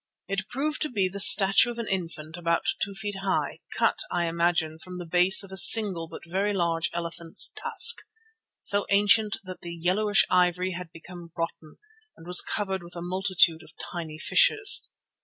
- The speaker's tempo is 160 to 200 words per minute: Yes, average, 175 wpm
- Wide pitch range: No, average, 2.9 semitones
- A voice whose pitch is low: No, medium, 185 Hz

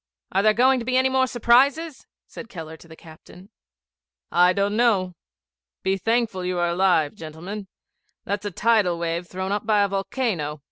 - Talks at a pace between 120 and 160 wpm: No, average, 175 wpm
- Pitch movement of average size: Yes, average, 4.9 semitones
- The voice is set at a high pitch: Yes, high, 195 Hz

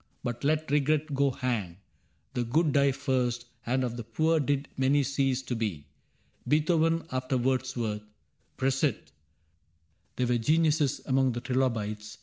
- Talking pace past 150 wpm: No, slow, 135 wpm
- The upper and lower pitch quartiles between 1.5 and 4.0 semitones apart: Yes, average, 3.0 semitones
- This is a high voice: No, low, 130 Hz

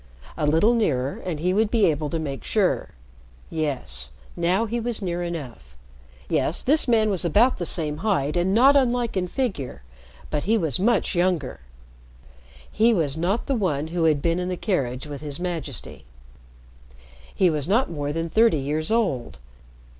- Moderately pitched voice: Yes, medium, 170 Hz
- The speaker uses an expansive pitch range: Yes, wide, 6.4 semitones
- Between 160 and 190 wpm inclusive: Yes, average, 170 wpm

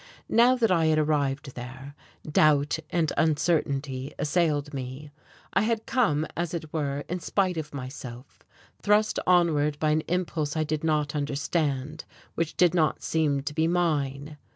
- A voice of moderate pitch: Yes, medium, 155 Hz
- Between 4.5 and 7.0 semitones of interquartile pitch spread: No, average, 2.9 semitones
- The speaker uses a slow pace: No, average, 155 wpm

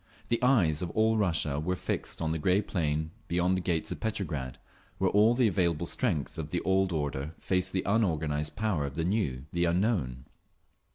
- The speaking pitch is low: Yes, very low, 85 Hz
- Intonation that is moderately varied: Yes, average, 4.4 semitones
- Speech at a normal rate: Yes, average, 185 wpm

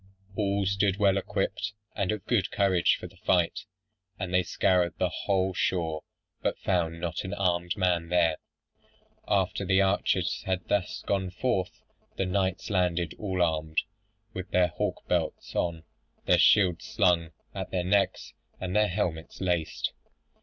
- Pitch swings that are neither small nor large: No, narrow, 2.0 semitones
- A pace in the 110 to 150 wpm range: Yes, average, 145 wpm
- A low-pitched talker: Yes, very low, 90 Hz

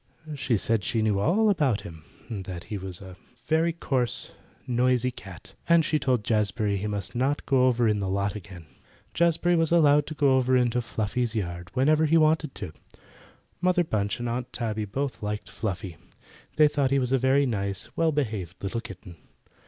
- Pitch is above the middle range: No, low, 120 Hz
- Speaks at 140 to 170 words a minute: No, average, 185 wpm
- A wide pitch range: Yes, wide, 6.0 semitones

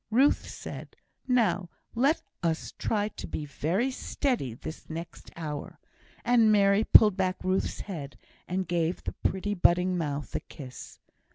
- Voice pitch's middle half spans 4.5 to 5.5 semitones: Yes, average, 4.8 semitones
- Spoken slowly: No, average, 150 wpm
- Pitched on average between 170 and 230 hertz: Yes, medium, 185 Hz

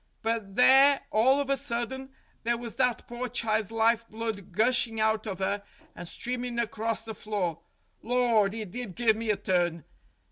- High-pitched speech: Yes, high, 225 Hz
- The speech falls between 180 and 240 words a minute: No, average, 170 wpm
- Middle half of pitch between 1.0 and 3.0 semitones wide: Yes, narrow, 2.5 semitones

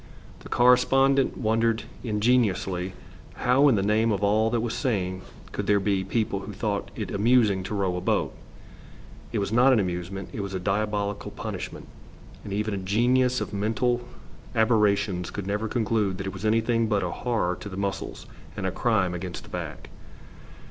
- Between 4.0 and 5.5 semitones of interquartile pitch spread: No, average, 2.9 semitones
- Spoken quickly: No, average, 175 wpm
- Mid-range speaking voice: No, low, 105 Hz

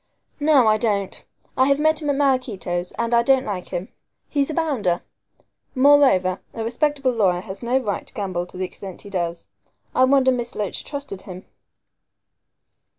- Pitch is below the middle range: No, high, 235 Hz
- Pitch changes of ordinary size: No, wide, 6.4 semitones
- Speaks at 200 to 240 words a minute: No, average, 170 wpm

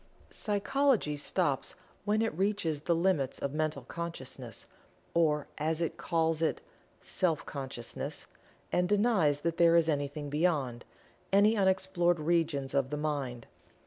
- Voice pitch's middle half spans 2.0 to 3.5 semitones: No, average, 3.9 semitones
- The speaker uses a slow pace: Yes, slow, 130 wpm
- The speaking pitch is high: No, medium, 160 Hz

